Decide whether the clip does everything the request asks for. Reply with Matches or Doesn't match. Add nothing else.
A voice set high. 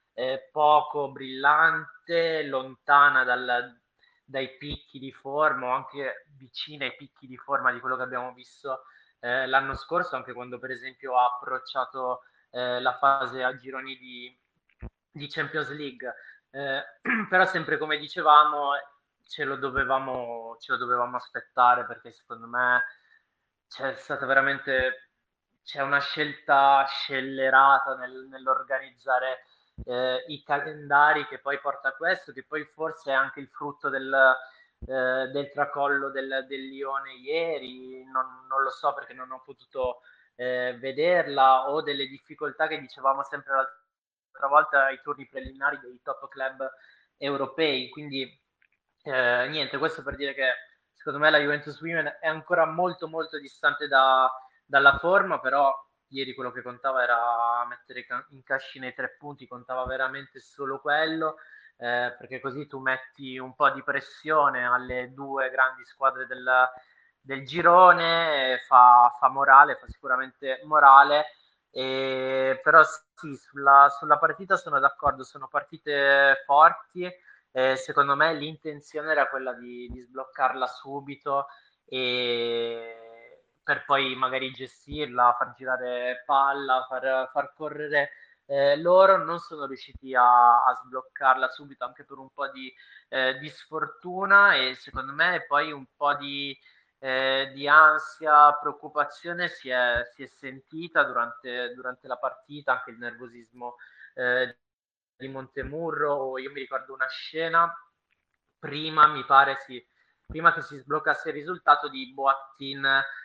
Doesn't match